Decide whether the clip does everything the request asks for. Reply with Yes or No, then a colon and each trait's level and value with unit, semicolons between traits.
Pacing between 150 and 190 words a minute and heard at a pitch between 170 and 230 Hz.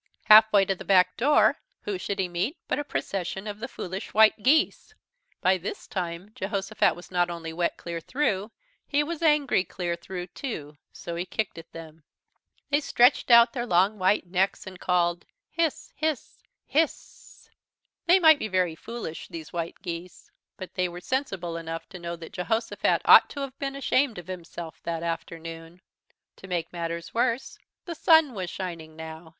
Yes: average, 175 wpm; medium, 185 Hz